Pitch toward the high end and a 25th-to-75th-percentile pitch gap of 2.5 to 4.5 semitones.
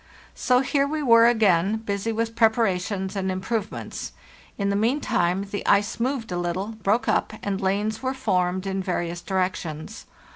Yes: high, 205 Hz; average, 3.4 semitones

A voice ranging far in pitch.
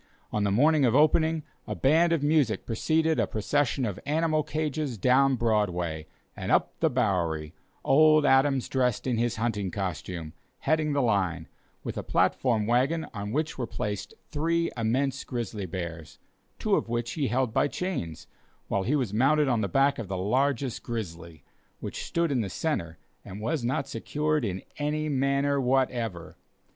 Yes: wide, 6.1 semitones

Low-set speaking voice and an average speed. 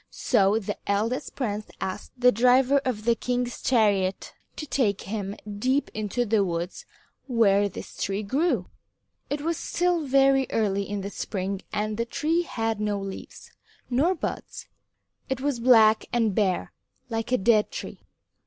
No: high, 225 Hz; average, 155 wpm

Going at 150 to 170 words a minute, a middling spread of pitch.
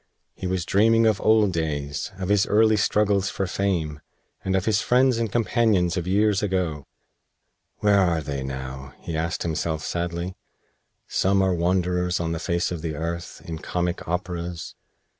Yes: average, 160 wpm; average, 3.3 semitones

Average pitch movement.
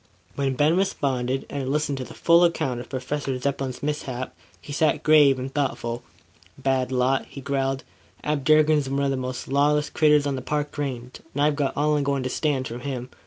No: narrow, 2.2 semitones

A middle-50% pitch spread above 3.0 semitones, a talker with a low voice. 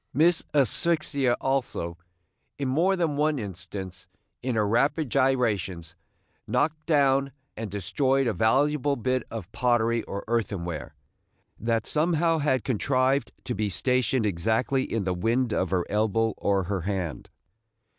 Yes: wide, 5.4 semitones; low, 120 Hz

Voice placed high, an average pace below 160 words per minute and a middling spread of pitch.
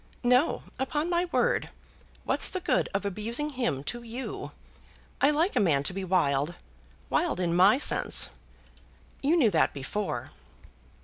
No: high, 230 Hz; average, 145 wpm; wide, 8.6 semitones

